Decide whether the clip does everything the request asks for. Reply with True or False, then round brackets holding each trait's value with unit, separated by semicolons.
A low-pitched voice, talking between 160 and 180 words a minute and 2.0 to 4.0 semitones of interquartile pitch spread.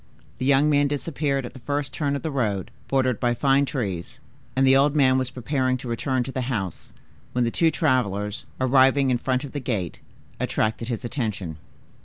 False (130 Hz; 195 wpm; 2.8 semitones)